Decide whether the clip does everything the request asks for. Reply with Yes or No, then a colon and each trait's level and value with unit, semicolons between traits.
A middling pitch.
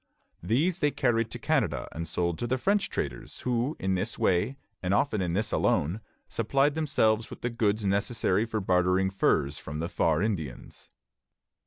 No: low, 105 Hz